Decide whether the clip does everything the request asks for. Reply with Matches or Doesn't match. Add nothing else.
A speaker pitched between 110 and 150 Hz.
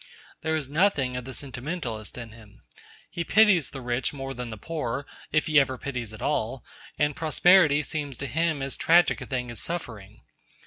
Matches